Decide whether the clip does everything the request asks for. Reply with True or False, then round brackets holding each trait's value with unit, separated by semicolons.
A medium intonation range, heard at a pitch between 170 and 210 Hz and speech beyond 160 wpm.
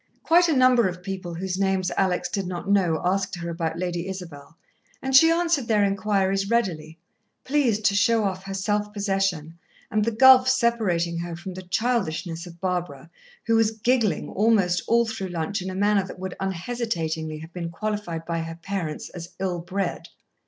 True (4.0 semitones; 190 Hz; 180 wpm)